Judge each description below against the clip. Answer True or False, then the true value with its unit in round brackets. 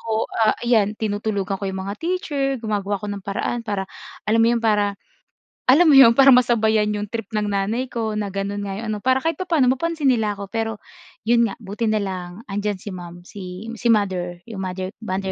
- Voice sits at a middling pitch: False (215 Hz)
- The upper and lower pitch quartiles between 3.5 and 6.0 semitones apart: False (2.9 semitones)